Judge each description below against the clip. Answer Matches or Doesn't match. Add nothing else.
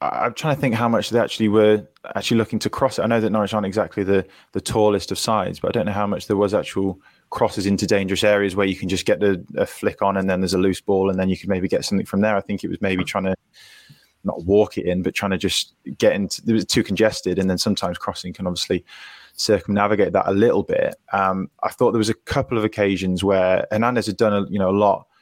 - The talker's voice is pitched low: Matches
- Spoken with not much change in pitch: Matches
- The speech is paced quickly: Matches